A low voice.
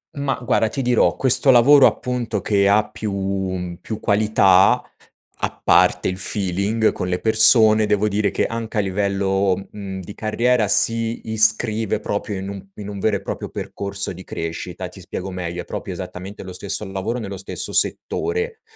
Yes: low, 105 Hz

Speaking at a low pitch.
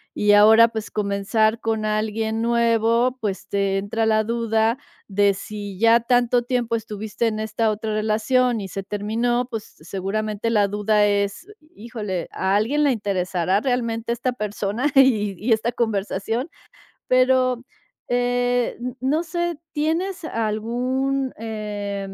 No: high, 220 Hz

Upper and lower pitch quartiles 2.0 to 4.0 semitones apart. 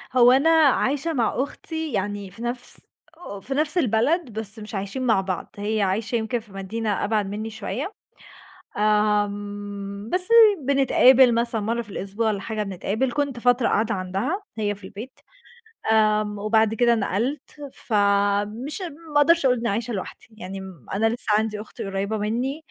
Yes: average, 3.6 semitones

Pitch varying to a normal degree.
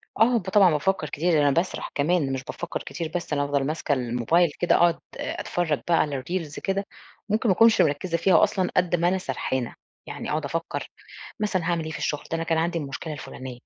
Yes: average, 3.8 semitones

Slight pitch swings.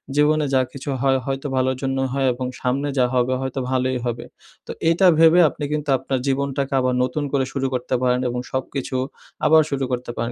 Yes: narrow, 1.6 semitones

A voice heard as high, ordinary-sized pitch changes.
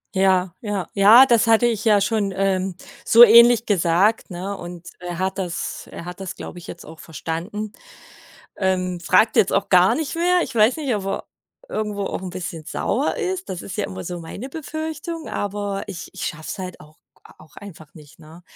Yes: high, 195 Hz; average, 4.2 semitones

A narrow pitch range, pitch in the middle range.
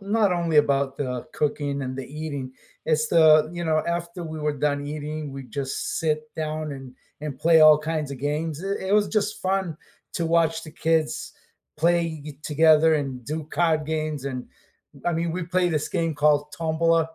Yes: narrow, 2.2 semitones; medium, 155 Hz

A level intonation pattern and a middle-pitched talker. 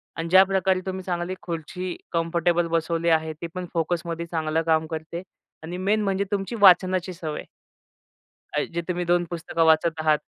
Yes: narrow, 2.0 semitones; medium, 170 Hz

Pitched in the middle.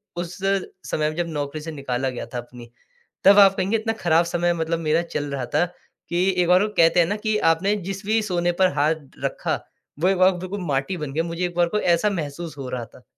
Yes: medium, 170 Hz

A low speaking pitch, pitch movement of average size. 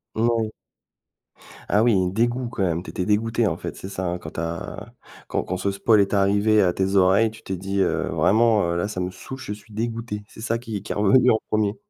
Yes: low, 105 Hz; average, 3.0 semitones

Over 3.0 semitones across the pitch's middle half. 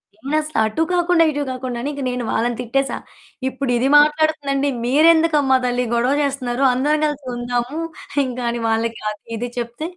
Yes: average, 3.6 semitones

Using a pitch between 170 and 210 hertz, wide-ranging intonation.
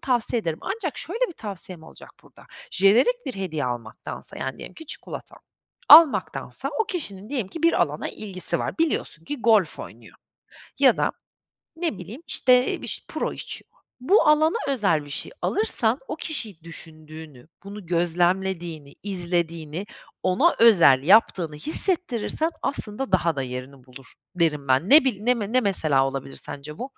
Yes: high, 190 Hz; wide, 8.3 semitones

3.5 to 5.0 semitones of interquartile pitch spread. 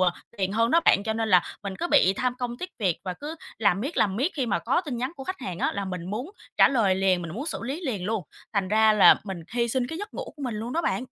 No: wide, 5.6 semitones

